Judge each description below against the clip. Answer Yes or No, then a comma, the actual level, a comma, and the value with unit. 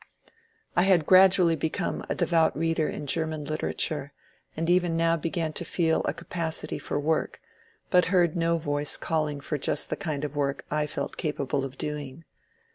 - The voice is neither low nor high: Yes, medium, 160 Hz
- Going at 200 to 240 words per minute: No, average, 175 wpm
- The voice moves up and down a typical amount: No, narrow, 2.2 semitones